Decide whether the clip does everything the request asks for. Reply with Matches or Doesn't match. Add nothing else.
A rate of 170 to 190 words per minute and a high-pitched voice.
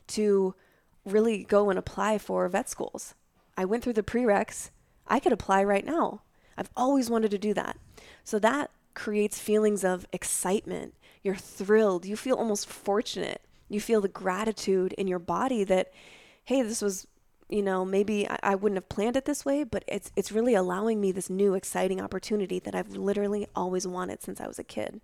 Matches